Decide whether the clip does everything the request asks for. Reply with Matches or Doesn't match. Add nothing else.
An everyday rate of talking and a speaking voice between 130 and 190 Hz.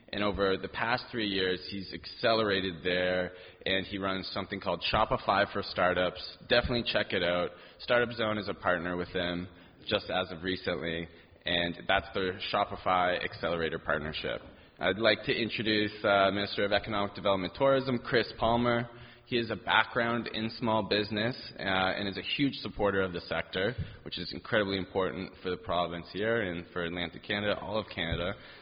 Doesn't match